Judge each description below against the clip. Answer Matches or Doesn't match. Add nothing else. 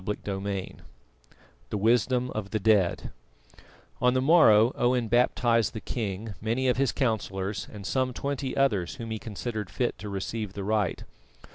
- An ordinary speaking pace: Matches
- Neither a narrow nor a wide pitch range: Matches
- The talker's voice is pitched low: Matches